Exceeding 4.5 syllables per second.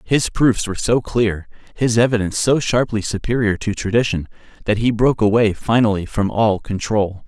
Yes: 5.2 syllables/s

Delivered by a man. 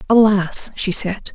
No: female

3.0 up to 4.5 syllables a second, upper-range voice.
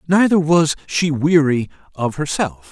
No: 4.1 syllables/s; medium, 150 Hz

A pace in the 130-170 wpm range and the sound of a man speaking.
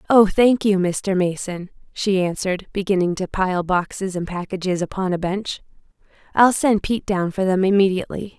No: average, 165 wpm; female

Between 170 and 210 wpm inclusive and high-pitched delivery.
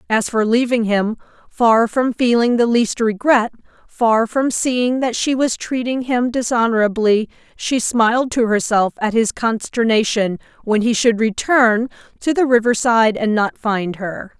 No: average, 155 wpm; high, 230 Hz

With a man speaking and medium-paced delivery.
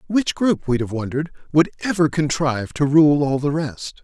Yes: male; average, 195 wpm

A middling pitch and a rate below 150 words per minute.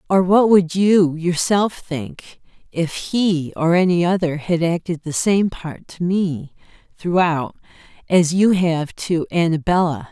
Yes: medium, 170 Hz; average, 140 wpm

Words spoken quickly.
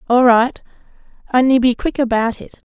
No: average, 155 wpm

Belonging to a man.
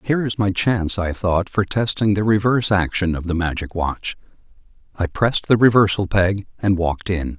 Yes: male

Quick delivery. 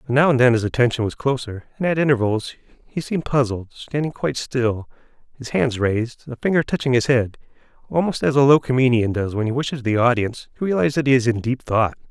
Yes: fast, 220 wpm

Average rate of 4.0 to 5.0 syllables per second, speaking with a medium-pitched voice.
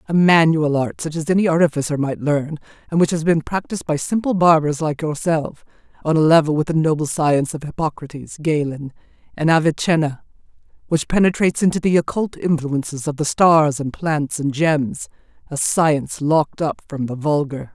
No: 5.3 syllables/s; medium, 155 Hz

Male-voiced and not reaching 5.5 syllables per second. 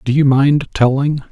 Yes: male; 4.4 syllables/s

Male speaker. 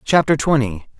Yes: male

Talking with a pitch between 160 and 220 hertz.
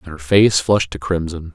No: very low, 85 Hz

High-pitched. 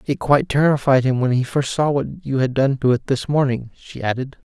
No: low, 135 Hz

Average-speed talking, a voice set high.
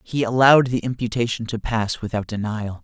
No: average, 170 wpm; low, 115 Hz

